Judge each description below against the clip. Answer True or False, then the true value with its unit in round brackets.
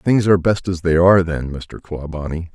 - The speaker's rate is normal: False (210 wpm)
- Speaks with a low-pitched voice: True (85 Hz)